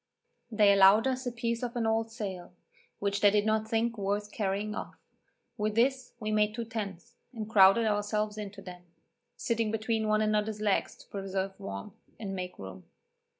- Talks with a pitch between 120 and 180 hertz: No, high, 210 Hz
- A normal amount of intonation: No, narrow, 2.1 semitones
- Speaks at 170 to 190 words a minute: Yes, average, 175 wpm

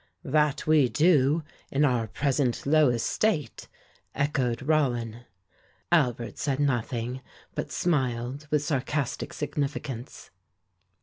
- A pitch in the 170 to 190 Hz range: No, medium, 140 Hz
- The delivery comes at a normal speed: No, slow, 100 wpm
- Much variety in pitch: No, average, 3.5 semitones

